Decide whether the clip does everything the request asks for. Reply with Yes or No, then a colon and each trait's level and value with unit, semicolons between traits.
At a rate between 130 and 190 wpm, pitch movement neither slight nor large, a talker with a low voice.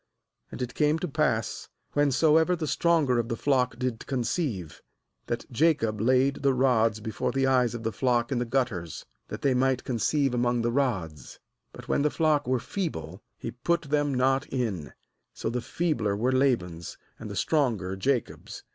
Yes: average, 170 wpm; average, 3.8 semitones; low, 125 Hz